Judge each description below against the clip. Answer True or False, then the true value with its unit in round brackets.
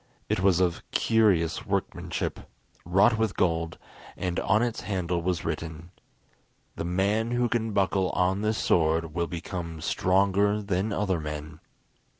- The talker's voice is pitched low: True (90 Hz)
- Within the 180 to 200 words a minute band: False (140 wpm)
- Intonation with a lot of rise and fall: False (3.6 semitones)